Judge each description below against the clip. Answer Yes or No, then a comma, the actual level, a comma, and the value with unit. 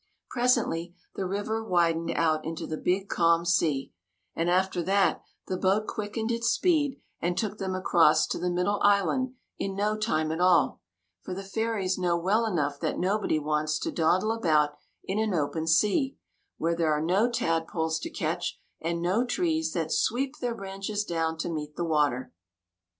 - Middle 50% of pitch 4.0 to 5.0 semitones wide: Yes, average, 4.7 semitones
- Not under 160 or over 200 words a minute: Yes, average, 170 wpm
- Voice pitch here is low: No, medium, 185 Hz